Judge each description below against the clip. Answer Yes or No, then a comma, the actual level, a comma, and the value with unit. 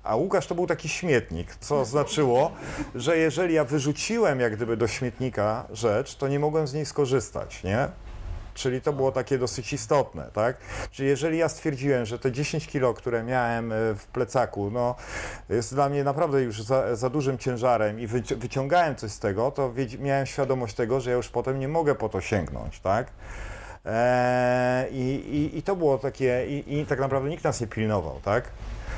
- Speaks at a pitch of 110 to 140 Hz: Yes, low, 130 Hz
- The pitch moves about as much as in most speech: Yes, average, 3.6 semitones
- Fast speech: Yes, fast, 180 wpm